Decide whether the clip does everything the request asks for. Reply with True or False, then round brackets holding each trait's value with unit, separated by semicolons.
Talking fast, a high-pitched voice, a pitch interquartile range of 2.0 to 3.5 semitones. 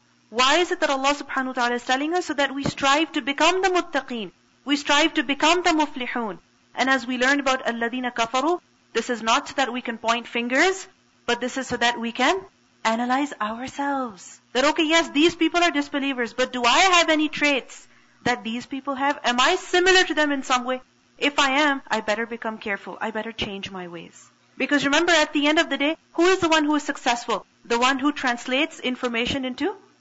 False (215 wpm; 275 Hz; 4.1 semitones)